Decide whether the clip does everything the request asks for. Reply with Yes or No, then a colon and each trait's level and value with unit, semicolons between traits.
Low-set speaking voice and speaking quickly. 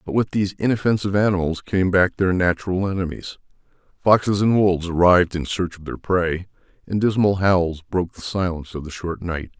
No: very low, 90 Hz; average, 180 wpm